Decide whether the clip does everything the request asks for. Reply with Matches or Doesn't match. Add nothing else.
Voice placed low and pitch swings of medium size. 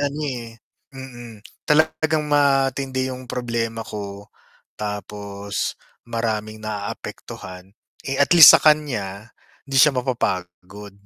Matches